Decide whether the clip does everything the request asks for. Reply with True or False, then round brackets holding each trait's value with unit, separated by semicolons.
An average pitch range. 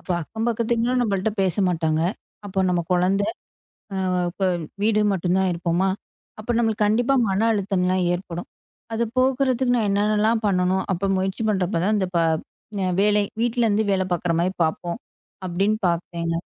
True (3.4 semitones)